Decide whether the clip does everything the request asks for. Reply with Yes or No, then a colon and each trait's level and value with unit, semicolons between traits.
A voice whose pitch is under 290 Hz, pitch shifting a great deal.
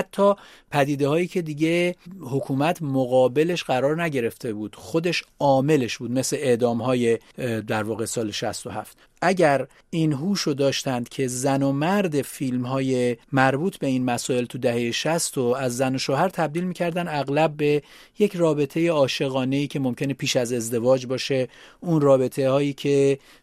No: medium, 140 Hz; average, 3.9 semitones